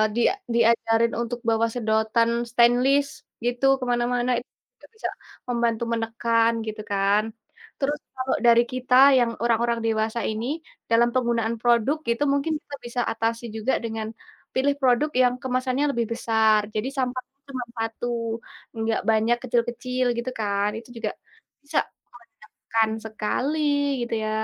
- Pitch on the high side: Yes, high, 235 Hz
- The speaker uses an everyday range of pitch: No, narrow, 2.0 semitones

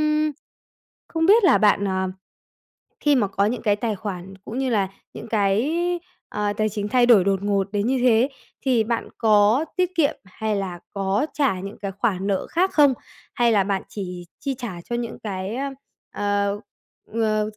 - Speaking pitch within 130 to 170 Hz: No, high, 215 Hz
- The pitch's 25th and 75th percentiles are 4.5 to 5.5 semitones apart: No, average, 4.0 semitones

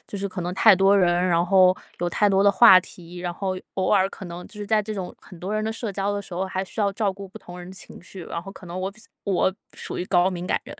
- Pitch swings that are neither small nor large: No, narrow, 2.0 semitones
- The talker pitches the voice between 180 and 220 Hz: Yes, high, 190 Hz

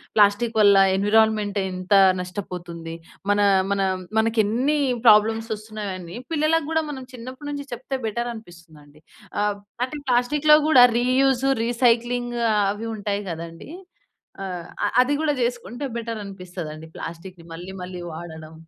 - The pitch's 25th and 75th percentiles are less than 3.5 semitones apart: No, average, 5.1 semitones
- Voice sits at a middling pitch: No, high, 215 Hz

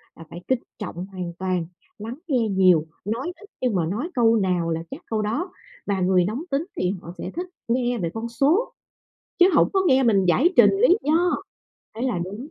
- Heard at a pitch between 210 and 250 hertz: Yes, high, 225 Hz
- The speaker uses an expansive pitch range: Yes, wide, 6.5 semitones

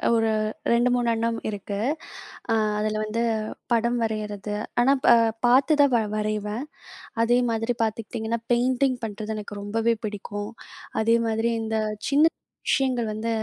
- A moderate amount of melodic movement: No, narrow, 2.0 semitones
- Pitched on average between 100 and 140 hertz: No, high, 225 Hz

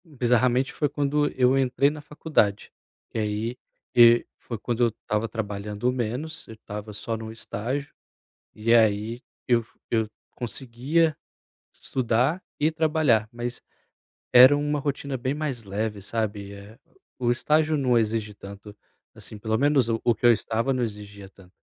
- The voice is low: Yes, low, 120 Hz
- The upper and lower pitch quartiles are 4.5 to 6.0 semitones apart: No, average, 4.1 semitones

